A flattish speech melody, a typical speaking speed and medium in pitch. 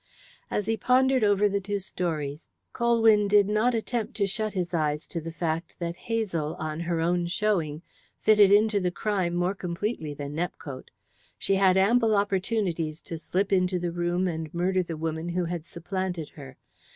No: average, 3.8 semitones; average, 175 wpm; medium, 180 Hz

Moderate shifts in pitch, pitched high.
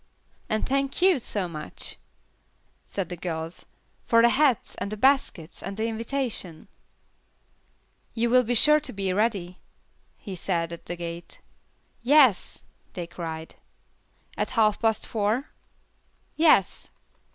No: wide, 5.9 semitones; high, 215 Hz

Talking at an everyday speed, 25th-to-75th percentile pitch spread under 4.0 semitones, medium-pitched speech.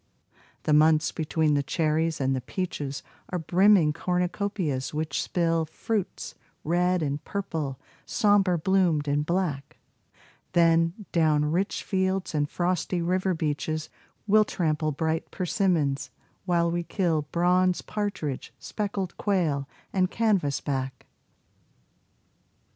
No: slow, 115 wpm; average, 3.6 semitones; medium, 165 Hz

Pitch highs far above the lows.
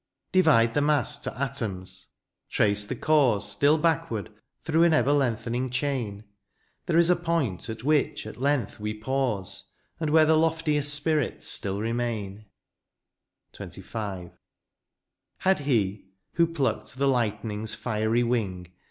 Yes: wide, 5.9 semitones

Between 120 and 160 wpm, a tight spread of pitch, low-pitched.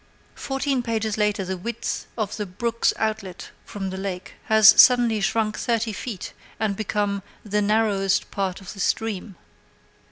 No: average, 150 wpm; narrow, 2.3 semitones; high, 210 Hz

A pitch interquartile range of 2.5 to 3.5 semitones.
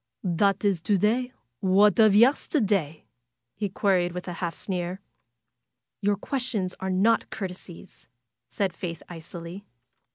Yes: average, 2.9 semitones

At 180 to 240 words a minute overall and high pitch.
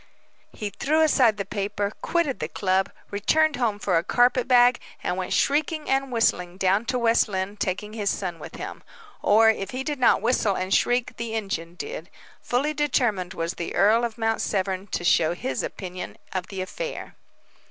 Yes: average, 185 wpm; high, 210 Hz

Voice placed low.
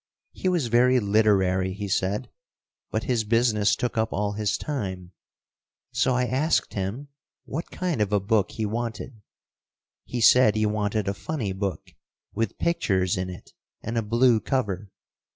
Yes: low, 110 Hz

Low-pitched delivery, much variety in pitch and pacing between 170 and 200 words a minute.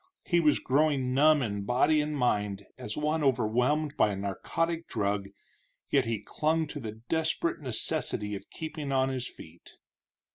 No: low, 130 Hz; wide, 6.2 semitones; average, 155 wpm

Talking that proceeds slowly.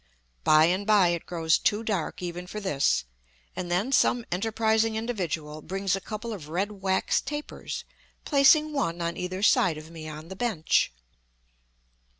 No: average, 155 wpm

